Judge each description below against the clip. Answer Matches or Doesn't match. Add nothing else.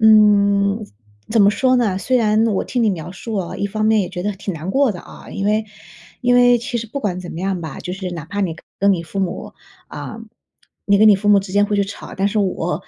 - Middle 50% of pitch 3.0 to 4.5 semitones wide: Doesn't match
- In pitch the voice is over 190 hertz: Matches